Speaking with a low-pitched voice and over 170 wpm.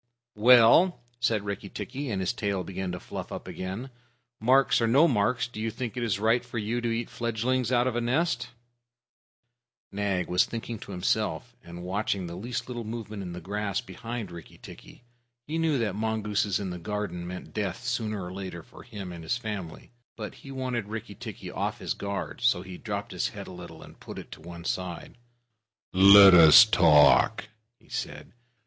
Yes: low, 105 Hz; average, 195 wpm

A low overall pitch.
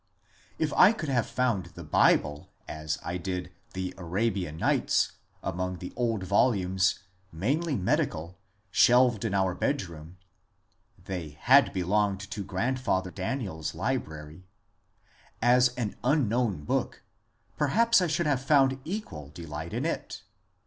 Yes: low, 100 Hz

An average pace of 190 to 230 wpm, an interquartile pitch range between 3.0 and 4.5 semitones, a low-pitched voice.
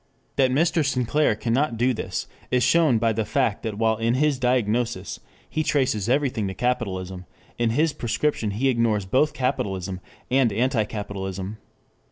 No: average, 155 wpm; average, 3.9 semitones; low, 115 Hz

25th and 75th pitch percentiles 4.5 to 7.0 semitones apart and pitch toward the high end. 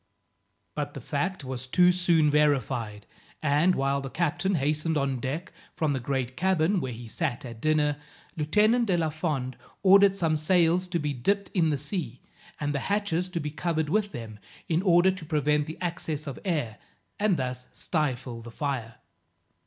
No: average, 4.8 semitones; medium, 155 Hz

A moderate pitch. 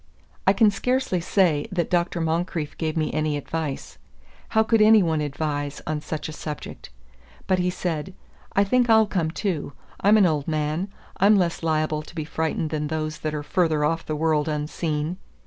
Yes: medium, 160 Hz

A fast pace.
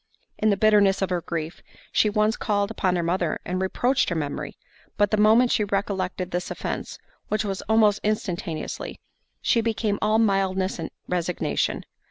No: average, 160 wpm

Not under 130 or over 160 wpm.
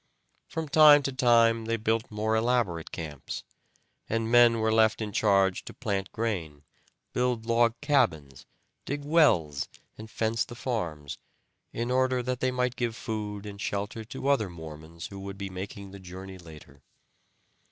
Yes: average, 155 wpm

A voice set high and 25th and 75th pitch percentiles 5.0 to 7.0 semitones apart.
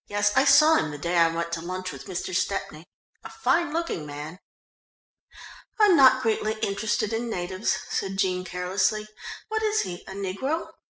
Yes: high, 195 Hz; average, 5.3 semitones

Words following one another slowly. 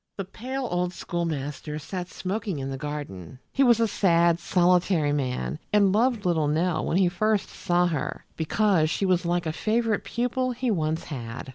No: average, 175 wpm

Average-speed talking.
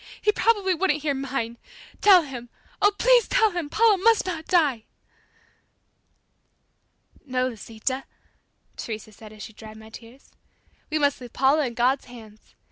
Yes: average, 145 wpm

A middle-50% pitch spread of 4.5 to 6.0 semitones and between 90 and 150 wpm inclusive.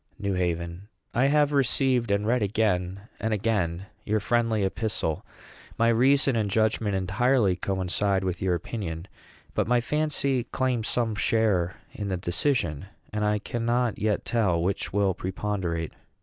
No: average, 4.1 semitones; average, 145 wpm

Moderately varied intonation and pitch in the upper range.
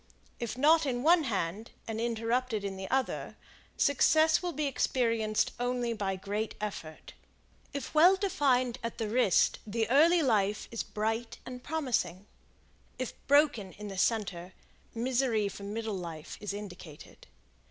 Yes: average, 4.3 semitones; high, 230 Hz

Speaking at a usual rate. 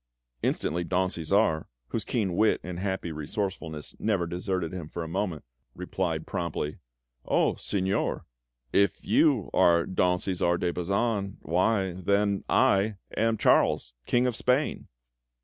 No: slow, 130 wpm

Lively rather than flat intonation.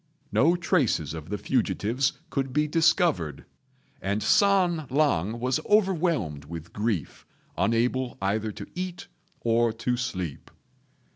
Yes: wide, 8.1 semitones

